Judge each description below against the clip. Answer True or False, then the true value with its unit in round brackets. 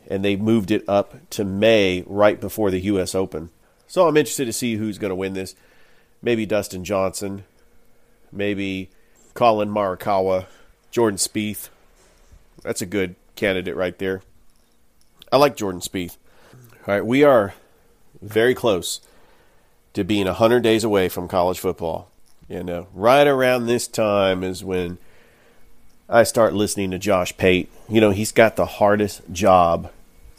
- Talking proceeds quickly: False (150 wpm)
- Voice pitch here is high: False (100 Hz)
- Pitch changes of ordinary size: True (3.0 semitones)